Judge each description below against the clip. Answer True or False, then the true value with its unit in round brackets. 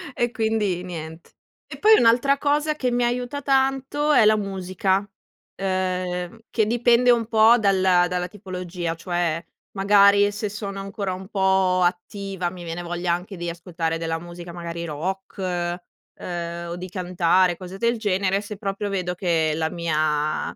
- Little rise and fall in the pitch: False (3.5 semitones)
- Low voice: False (190 Hz)